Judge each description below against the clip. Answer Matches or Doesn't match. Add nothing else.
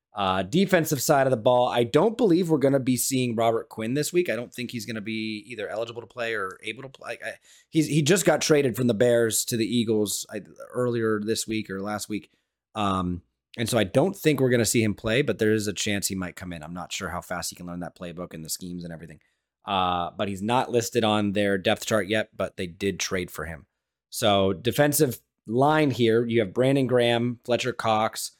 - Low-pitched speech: Matches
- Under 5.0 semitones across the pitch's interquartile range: Matches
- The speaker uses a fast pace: Matches